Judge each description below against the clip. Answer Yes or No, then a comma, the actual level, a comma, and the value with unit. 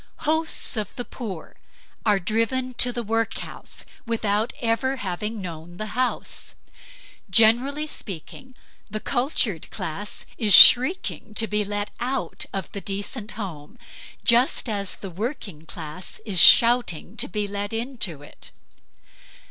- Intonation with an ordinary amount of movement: Yes, average, 3.9 semitones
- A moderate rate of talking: No, slow, 130 wpm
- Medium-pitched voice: No, high, 215 Hz